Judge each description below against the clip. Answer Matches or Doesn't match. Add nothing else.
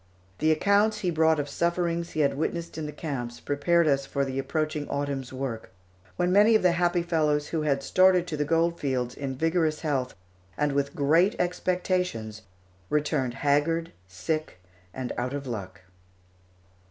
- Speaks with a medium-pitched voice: Matches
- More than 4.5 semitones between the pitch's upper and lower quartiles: Doesn't match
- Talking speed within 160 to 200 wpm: Matches